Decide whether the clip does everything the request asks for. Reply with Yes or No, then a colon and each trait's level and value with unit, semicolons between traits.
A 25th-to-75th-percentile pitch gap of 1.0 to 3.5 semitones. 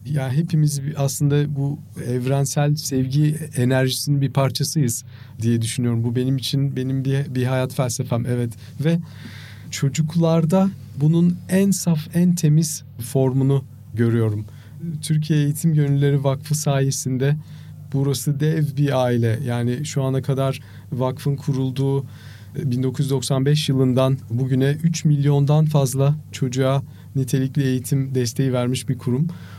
Yes: narrow, 2.5 semitones